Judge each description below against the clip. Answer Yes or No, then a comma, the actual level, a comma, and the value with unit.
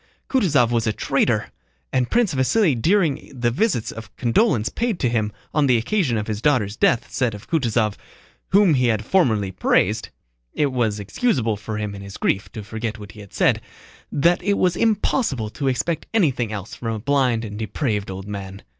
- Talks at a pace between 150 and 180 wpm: No, average, 190 wpm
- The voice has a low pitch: Yes, low, 120 Hz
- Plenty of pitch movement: Yes, wide, 6.1 semitones